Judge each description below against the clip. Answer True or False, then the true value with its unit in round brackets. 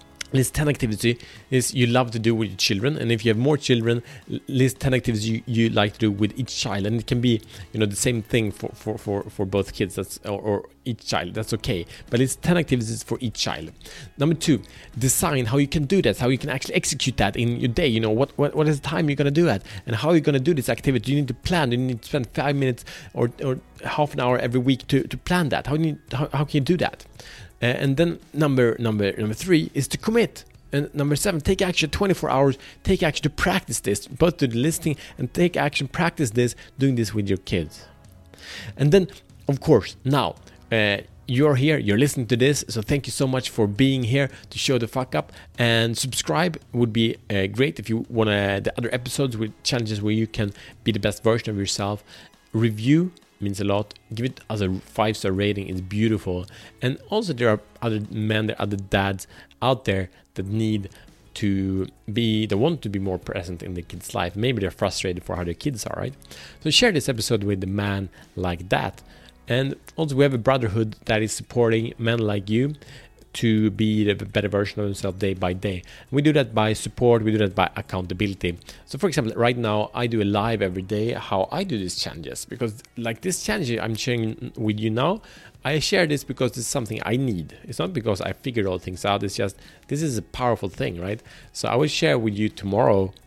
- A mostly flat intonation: False (4.8 semitones)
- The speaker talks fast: True (230 wpm)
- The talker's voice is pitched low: True (115 Hz)